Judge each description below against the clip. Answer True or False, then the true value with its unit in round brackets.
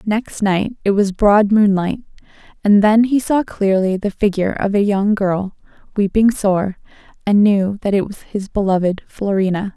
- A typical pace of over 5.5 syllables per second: False (4.5 syllables/s)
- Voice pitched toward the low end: False (200 Hz)